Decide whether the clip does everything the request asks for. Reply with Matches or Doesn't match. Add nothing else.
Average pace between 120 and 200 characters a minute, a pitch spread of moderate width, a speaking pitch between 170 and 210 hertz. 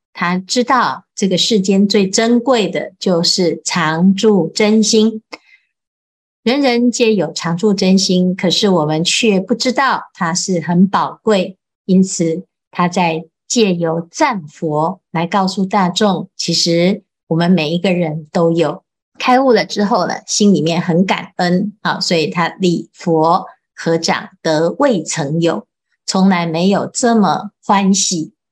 Matches